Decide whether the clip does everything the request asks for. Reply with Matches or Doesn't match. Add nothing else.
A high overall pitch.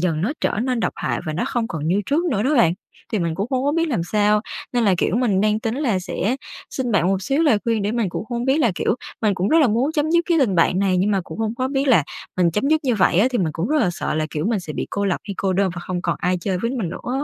Matches